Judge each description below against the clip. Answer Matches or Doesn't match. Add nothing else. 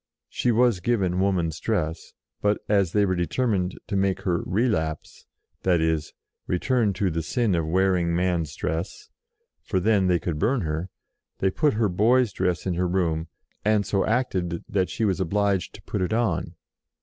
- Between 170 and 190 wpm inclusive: Matches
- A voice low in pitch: Matches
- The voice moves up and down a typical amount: Matches